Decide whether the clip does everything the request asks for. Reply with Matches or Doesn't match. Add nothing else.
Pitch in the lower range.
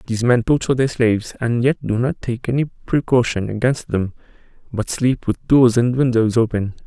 Matches